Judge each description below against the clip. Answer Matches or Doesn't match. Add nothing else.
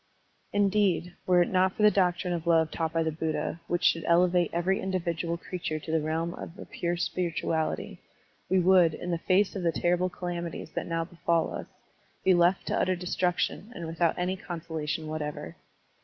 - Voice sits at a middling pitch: Matches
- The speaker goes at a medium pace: Matches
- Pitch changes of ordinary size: Doesn't match